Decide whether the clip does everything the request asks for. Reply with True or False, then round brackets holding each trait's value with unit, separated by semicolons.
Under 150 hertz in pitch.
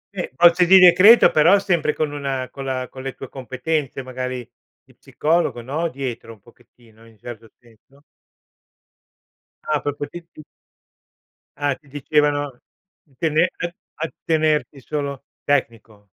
True (140 Hz)